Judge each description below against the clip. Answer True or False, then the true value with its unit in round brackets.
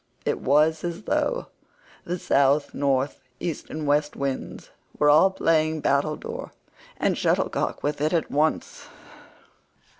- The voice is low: False (150 Hz)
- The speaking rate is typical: False (125 wpm)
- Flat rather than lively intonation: True (2.1 semitones)